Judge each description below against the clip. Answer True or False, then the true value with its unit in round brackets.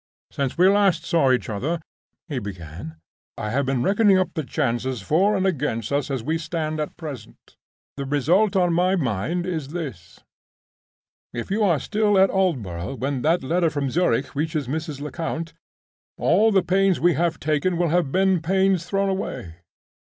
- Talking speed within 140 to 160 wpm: False (175 wpm)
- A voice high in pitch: False (160 Hz)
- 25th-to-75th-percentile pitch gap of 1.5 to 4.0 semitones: False (5.5 semitones)